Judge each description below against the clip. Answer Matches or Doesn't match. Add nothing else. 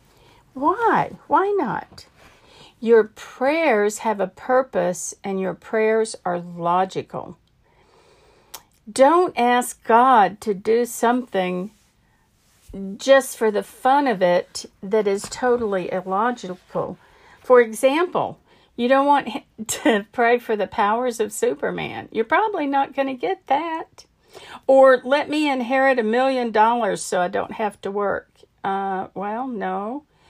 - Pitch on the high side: Matches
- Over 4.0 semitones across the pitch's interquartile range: Matches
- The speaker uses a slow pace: Matches